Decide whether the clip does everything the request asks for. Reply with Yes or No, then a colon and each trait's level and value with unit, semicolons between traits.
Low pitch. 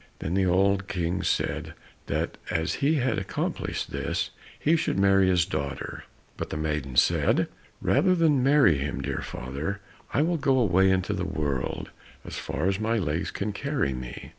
Yes: very low, 95 Hz